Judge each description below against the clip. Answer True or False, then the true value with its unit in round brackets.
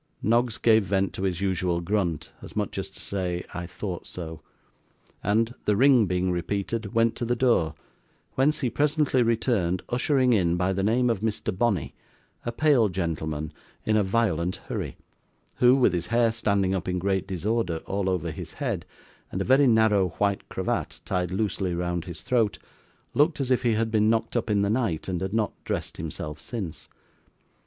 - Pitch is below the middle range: True (100 Hz)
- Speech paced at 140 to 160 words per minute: False (180 wpm)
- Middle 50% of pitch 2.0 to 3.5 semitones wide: False (4.3 semitones)